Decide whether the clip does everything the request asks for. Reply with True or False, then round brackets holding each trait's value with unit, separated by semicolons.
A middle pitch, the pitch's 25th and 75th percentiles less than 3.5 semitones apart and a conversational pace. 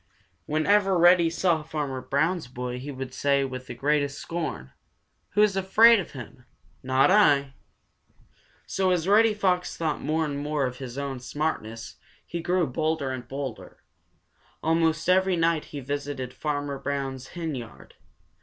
False (150 Hz; 4.5 semitones; 145 wpm)